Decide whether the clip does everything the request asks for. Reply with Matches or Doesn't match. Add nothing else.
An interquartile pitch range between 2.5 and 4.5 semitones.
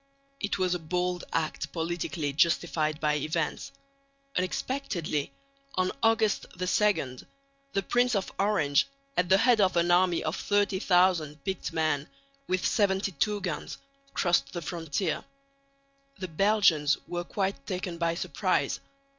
Matches